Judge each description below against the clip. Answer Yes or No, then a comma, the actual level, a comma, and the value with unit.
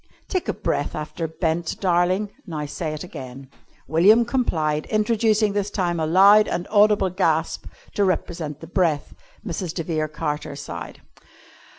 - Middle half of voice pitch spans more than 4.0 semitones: Yes, average, 4.7 semitones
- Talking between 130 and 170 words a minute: Yes, average, 150 wpm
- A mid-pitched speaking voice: Yes, medium, 175 Hz